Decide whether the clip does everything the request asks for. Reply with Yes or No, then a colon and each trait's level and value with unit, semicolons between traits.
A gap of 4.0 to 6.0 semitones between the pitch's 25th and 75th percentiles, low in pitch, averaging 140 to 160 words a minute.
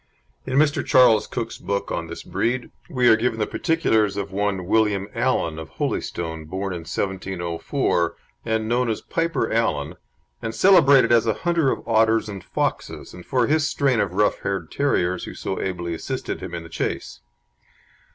No: wide, 5.5 semitones; low, 110 Hz; average, 170 wpm